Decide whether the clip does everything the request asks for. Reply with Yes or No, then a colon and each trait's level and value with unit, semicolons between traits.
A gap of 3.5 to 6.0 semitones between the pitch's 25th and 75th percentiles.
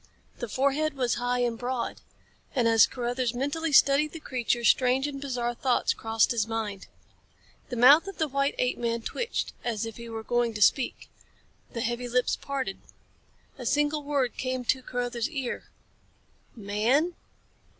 No: average, 2.9 semitones